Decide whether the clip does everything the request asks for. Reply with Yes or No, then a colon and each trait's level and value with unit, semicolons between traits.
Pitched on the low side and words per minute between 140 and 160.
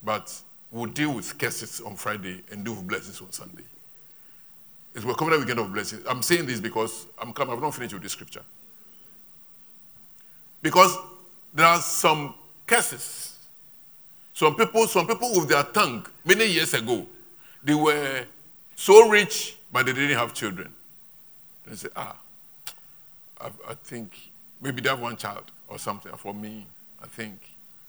Yes: low, 115 Hz; average, 155 wpm